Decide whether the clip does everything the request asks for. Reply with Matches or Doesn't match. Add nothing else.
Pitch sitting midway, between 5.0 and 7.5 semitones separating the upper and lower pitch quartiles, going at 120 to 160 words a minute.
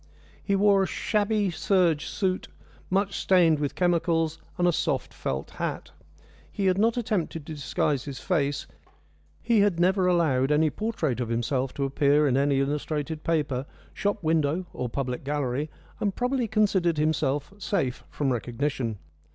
Matches